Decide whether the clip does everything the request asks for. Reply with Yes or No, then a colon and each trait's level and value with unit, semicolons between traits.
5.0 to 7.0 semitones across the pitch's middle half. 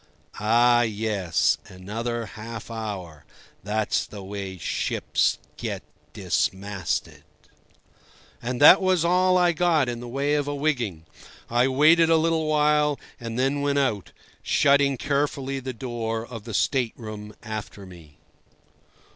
Yes: average, 5.3 semitones